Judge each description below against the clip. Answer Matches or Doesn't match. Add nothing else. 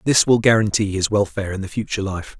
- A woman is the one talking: Doesn't match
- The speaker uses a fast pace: Matches